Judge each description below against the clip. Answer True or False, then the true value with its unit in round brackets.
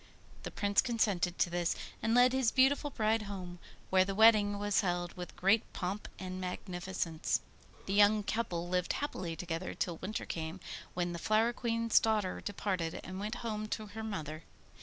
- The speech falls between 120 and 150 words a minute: False (170 wpm)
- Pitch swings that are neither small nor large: True (3.6 semitones)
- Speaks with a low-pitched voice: False (200 Hz)